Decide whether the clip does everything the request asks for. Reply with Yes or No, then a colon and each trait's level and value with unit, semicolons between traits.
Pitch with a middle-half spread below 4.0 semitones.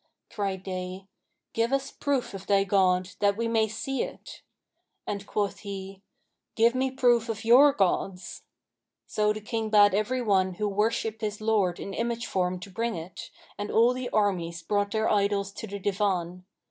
Yes: average, 2.9 semitones